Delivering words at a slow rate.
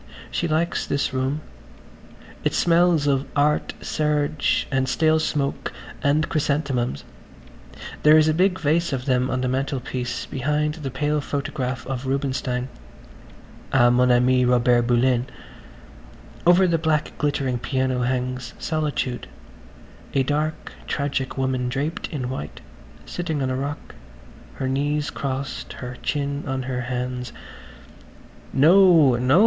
Yes: slow, 125 wpm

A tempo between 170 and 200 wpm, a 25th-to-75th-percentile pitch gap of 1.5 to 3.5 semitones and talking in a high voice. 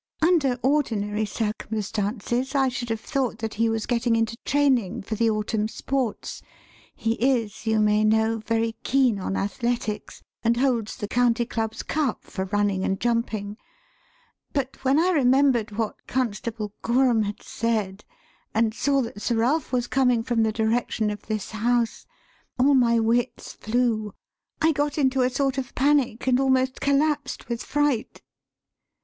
No: average, 155 wpm; average, 3.2 semitones; high, 235 Hz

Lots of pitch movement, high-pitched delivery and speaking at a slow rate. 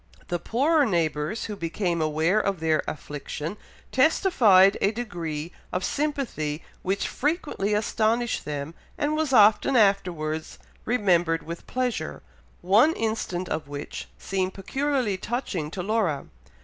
Yes: wide, 6.5 semitones; high, 195 Hz; slow, 125 wpm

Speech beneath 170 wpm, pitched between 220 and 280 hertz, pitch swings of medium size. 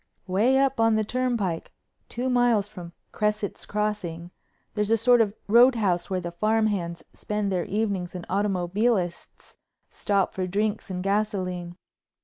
No: average, 140 wpm; high, 205 Hz; average, 3.4 semitones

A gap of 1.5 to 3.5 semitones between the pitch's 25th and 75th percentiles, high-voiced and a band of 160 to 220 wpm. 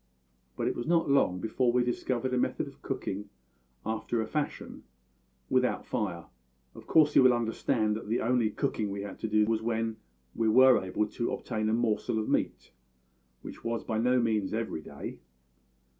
No: narrow, 2.5 semitones; low, 115 Hz; average, 180 wpm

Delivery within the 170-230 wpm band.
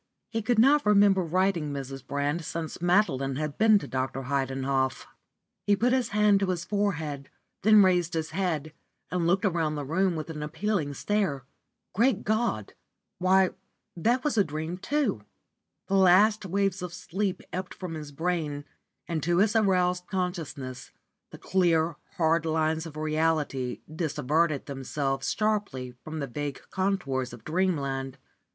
No: average, 150 wpm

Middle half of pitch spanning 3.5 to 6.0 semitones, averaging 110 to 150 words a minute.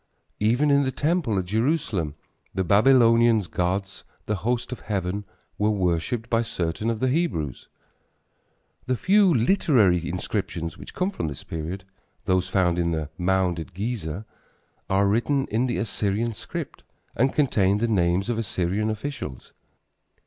Yes: average, 5.1 semitones; average, 145 wpm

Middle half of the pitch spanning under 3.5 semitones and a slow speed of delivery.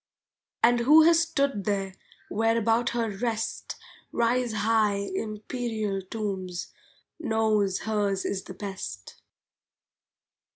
Yes: average, 2.9 semitones; slow, 100 wpm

